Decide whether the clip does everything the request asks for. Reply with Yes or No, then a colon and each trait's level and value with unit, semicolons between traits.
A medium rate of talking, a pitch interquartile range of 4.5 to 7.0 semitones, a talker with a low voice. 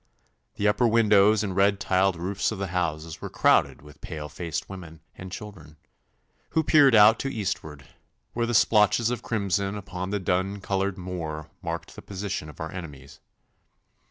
No: average, 165 wpm; average, 3.9 semitones; very low, 95 Hz